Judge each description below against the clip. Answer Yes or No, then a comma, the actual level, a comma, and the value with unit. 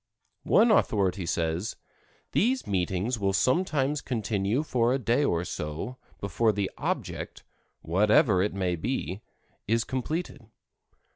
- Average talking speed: No, slow, 120 wpm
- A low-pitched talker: Yes, low, 110 Hz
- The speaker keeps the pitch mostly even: No, wide, 5.4 semitones